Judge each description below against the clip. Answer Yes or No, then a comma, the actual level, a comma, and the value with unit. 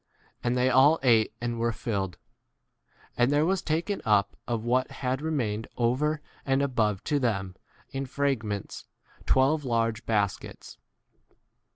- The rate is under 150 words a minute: Yes, average, 140 wpm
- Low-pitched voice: Yes, low, 125 Hz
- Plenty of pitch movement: No, average, 4.1 semitones